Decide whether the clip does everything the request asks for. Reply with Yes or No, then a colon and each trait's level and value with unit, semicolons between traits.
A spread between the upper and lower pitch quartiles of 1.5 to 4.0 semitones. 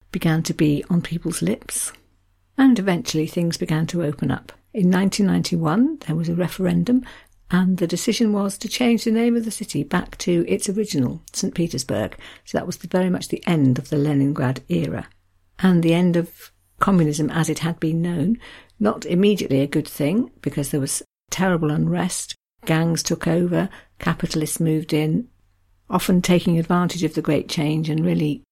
Yes: average, 3.2 semitones